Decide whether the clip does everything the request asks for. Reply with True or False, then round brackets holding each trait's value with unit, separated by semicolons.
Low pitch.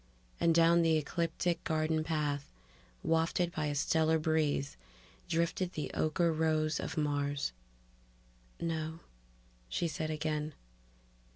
False (160 Hz)